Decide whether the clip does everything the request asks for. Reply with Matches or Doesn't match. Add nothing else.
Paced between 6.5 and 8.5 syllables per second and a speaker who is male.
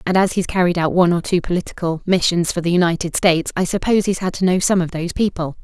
Doesn't match